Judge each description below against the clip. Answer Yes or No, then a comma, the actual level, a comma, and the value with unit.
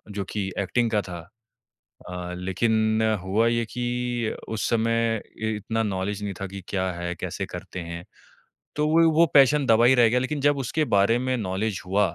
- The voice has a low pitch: Yes, low, 110 Hz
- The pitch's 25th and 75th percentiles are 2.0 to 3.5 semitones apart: No, average, 3.9 semitones